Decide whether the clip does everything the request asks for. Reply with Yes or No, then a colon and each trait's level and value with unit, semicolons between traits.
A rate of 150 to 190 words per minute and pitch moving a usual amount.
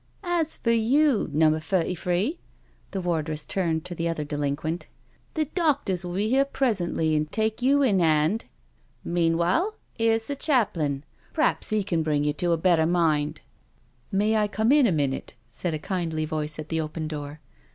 No: average, 185 wpm; wide, 6.2 semitones